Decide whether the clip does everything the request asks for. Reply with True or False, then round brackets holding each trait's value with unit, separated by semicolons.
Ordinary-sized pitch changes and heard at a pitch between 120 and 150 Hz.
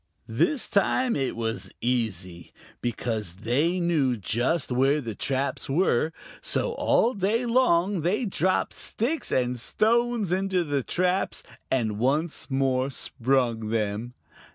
False (7.9 semitones; 135 Hz)